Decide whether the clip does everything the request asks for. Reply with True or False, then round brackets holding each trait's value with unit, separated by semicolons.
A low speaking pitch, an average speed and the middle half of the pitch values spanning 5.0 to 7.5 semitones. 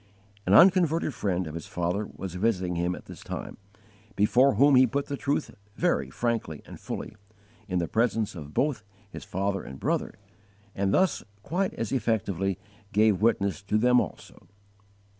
True (105 Hz; 160 wpm; 5.6 semitones)